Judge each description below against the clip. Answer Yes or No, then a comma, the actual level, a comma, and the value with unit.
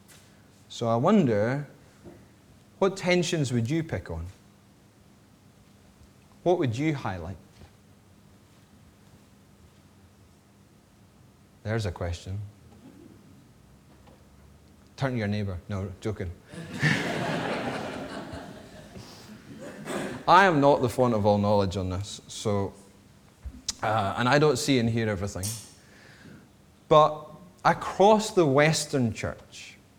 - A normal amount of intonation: Yes, average, 4.3 semitones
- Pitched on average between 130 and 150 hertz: No, low, 105 Hz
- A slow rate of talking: Yes, slow, 90 wpm